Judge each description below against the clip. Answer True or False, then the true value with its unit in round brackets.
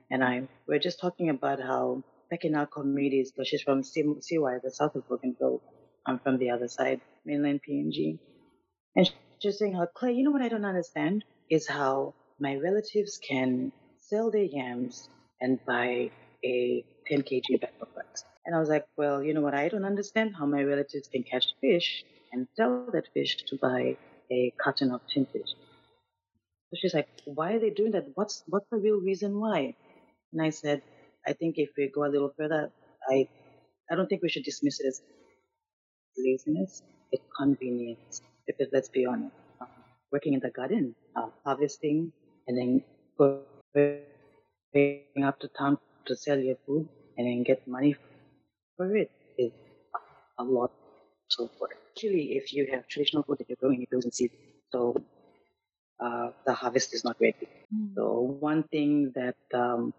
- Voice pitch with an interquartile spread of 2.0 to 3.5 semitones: False (4.0 semitones)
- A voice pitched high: False (140 Hz)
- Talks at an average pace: True (175 wpm)